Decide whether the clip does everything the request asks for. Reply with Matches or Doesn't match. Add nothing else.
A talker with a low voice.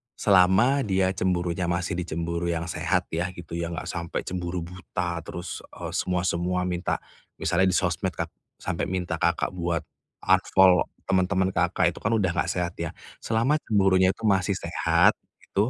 Matches